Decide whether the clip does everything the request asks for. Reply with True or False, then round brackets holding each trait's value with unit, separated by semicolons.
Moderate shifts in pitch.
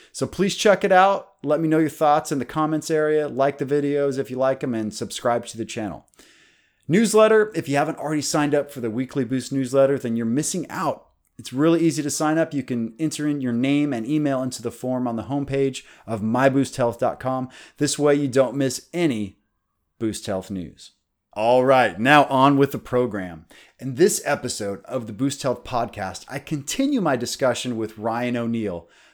True (4.1 semitones)